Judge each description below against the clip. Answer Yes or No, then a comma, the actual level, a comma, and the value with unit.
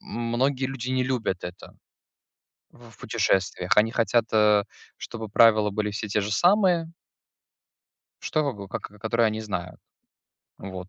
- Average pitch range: Yes, average, 3.5 semitones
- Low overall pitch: Yes, low, 110 Hz